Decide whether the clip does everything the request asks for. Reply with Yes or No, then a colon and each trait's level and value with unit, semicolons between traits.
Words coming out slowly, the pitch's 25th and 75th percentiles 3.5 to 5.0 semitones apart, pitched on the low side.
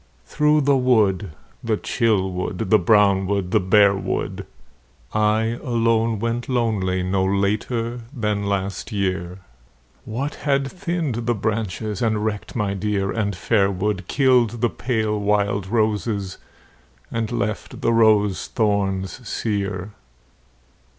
No: slow, 125 wpm; average, 2.8 semitones; low, 105 Hz